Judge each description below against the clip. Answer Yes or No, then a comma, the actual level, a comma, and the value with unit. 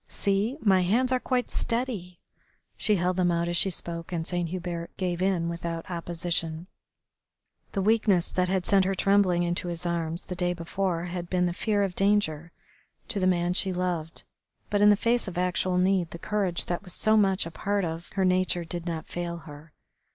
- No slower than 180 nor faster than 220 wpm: Yes, average, 195 wpm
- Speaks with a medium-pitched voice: Yes, medium, 180 Hz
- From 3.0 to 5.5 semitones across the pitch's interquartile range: No, narrow, 2.4 semitones